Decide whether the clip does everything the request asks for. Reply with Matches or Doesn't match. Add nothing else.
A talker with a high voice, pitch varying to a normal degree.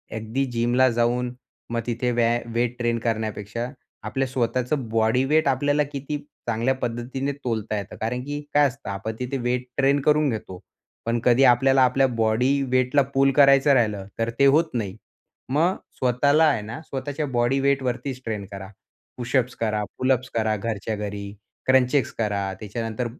Doesn't match